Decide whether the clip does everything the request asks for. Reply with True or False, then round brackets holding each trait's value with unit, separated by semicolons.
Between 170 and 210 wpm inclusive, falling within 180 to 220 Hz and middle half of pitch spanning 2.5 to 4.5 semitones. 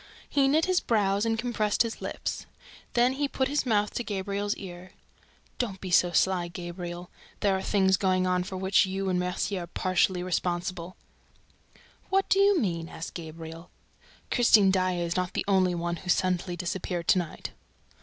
True (175 wpm; 185 Hz; 2.9 semitones)